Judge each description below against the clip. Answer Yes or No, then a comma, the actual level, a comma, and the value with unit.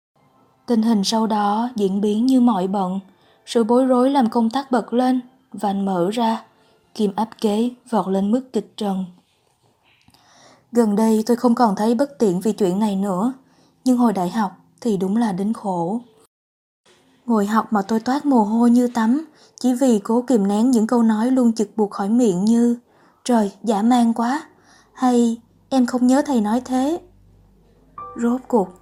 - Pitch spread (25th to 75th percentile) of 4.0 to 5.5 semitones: No, average, 2.8 semitones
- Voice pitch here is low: No, high, 230 Hz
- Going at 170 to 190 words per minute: Yes, average, 180 wpm